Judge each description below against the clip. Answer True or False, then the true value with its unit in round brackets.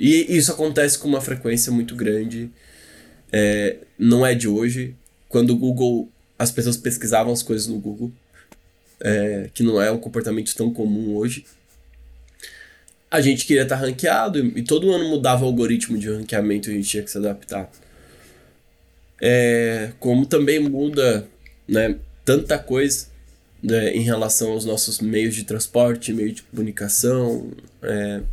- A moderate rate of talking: True (150 wpm)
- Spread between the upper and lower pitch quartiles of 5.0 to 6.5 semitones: False (3.2 semitones)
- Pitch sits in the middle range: False (115 Hz)